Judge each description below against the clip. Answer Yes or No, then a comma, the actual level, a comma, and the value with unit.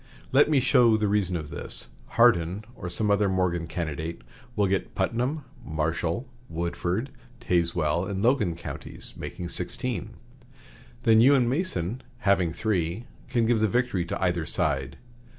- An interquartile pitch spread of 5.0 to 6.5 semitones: Yes, wide, 5.6 semitones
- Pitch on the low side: Yes, very low, 95 Hz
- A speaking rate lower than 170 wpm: Yes, average, 145 wpm